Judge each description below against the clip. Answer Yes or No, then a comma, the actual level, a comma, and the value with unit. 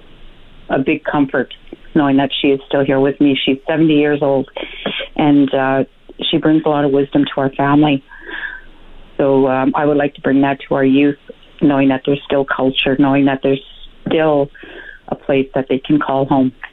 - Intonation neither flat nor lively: No, narrow, 1.2 semitones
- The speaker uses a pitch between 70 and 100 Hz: No, medium, 140 Hz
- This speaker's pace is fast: No, average, 190 wpm